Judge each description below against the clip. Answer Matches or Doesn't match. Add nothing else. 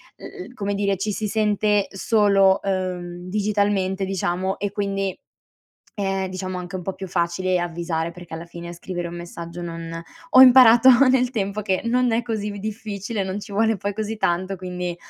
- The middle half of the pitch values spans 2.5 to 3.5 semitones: Matches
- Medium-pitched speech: Doesn't match